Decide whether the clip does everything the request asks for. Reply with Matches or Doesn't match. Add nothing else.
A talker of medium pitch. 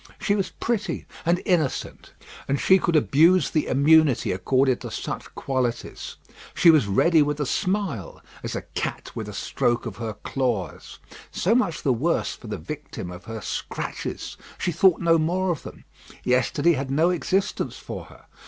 Matches